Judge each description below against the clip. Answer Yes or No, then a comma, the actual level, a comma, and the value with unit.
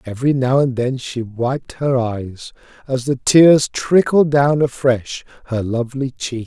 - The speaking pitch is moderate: No, low, 130 Hz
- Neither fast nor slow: Yes, average, 160 wpm